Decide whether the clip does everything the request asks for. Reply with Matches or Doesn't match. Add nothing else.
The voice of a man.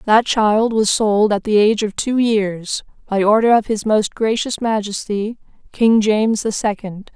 Doesn't match